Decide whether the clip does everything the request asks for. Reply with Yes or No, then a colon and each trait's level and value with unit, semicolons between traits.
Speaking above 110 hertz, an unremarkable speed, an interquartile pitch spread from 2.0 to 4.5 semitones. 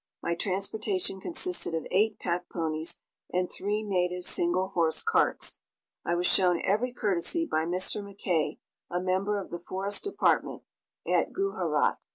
Yes: medium, 185 Hz; average, 145 wpm; average, 2.8 semitones